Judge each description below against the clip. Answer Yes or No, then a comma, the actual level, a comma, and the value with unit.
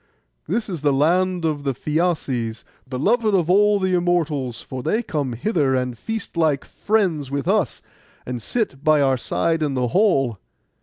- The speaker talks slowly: No, average, 165 wpm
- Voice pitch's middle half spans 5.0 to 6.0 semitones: Yes, wide, 5.6 semitones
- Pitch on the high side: No, medium, 155 Hz